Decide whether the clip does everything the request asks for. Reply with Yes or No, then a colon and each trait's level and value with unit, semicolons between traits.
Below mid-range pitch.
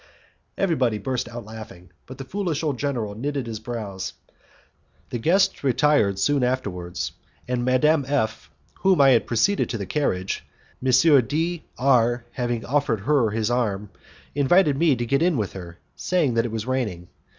Yes: low, 125 Hz